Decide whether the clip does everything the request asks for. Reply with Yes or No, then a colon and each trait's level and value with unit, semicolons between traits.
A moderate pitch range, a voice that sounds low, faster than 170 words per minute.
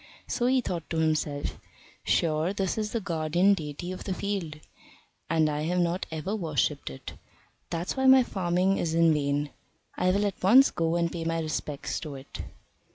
No: average, 3.7 semitones; medium, 170 Hz; average, 180 wpm